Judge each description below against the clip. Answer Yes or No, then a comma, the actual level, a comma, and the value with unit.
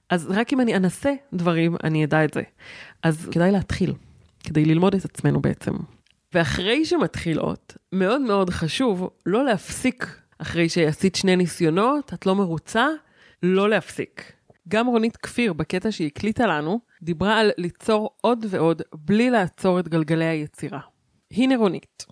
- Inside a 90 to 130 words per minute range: No, average, 145 wpm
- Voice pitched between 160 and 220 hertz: Yes, medium, 185 Hz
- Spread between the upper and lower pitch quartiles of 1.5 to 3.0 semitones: No, average, 5.0 semitones